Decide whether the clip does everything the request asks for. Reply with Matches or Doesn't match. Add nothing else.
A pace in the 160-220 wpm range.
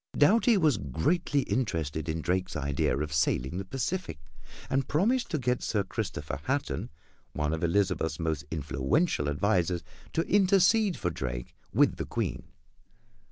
Doesn't match